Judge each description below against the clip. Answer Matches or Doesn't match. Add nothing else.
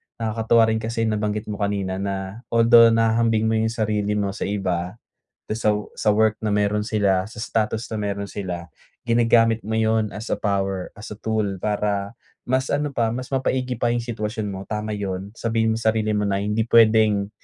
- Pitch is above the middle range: Doesn't match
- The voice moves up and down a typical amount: Doesn't match